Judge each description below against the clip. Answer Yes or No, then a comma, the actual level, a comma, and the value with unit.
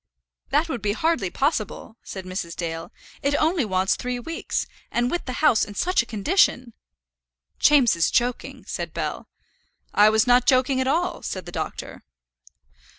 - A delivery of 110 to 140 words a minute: No, average, 160 wpm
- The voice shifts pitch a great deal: Yes, wide, 6.1 semitones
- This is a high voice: Yes, high, 245 Hz